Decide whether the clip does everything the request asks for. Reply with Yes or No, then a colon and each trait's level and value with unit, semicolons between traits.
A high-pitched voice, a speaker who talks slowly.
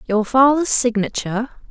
Yes: high, 235 Hz; slow, 105 wpm